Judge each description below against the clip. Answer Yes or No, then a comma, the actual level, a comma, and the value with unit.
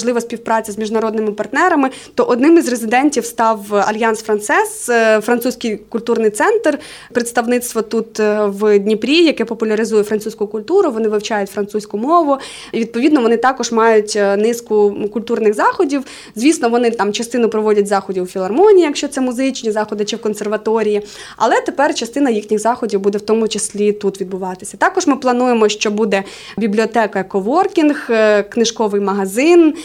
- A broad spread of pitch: No, average, 3.2 semitones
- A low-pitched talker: No, high, 225 Hz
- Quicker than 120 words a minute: Yes, average, 140 wpm